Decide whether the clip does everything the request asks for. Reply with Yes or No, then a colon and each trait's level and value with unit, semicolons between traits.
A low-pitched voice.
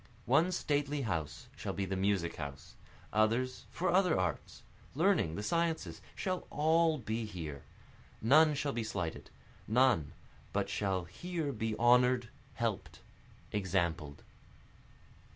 Yes: low, 110 Hz